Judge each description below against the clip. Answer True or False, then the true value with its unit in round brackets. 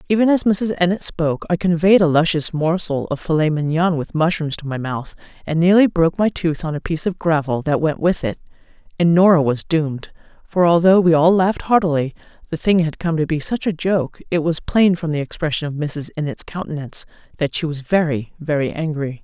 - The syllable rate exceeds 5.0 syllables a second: True (5.6 syllables/s)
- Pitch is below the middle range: False (165 Hz)